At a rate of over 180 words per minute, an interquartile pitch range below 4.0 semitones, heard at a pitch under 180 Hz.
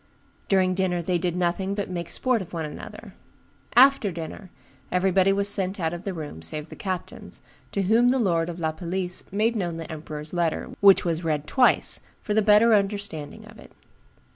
No: average, 190 wpm; average, 3.4 semitones; medium, 185 Hz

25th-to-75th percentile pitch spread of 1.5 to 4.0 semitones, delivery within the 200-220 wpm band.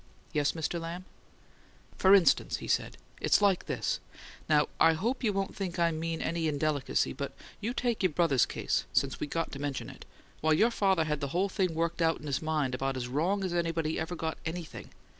Yes: average, 3.3 semitones; fast, 205 wpm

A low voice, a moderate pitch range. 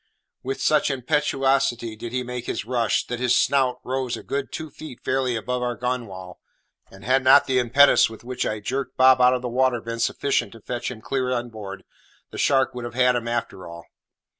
No: low, 125 Hz; narrow, 2.0 semitones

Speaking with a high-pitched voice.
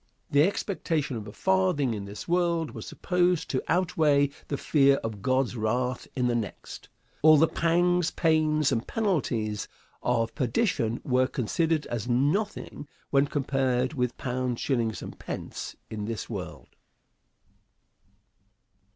No: low, 135 Hz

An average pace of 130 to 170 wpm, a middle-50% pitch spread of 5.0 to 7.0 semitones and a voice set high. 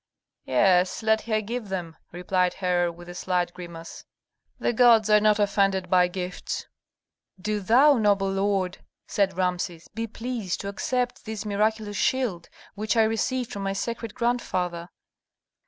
No: average, 145 wpm; average, 3.4 semitones; high, 200 Hz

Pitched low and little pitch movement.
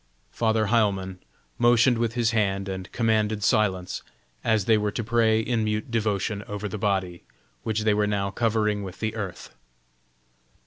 Yes: low, 105 Hz; narrow, 2.1 semitones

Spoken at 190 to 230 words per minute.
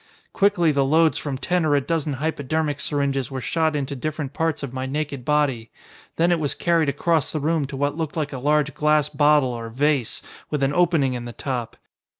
Yes: fast, 205 wpm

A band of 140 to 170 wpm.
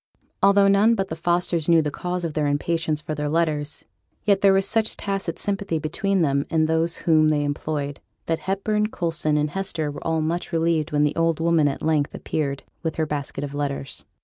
No: average, 200 wpm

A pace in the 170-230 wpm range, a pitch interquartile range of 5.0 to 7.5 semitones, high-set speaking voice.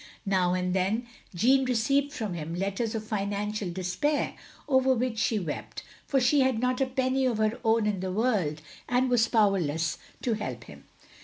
Yes: average, 175 wpm; wide, 5.4 semitones; high, 215 Hz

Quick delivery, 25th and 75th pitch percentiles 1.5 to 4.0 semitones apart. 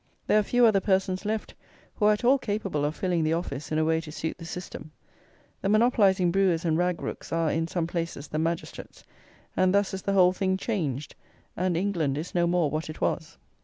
Yes: fast, 215 wpm; average, 3.3 semitones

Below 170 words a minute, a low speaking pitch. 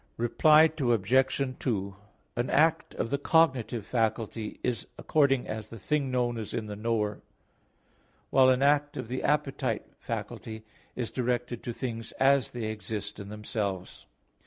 Yes: average, 145 wpm; low, 120 Hz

